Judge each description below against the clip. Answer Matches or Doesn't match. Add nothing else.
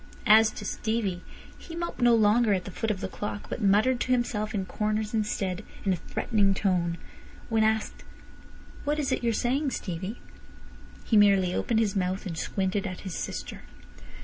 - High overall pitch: Matches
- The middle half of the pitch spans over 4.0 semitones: Doesn't match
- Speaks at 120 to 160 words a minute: Doesn't match